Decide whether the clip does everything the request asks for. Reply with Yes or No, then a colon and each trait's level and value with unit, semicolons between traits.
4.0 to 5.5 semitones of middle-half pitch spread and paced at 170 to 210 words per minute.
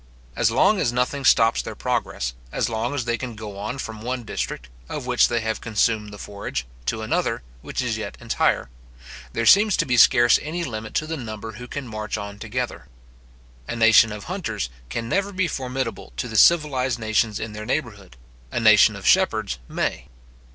No: average, 3.4 semitones; average, 190 wpm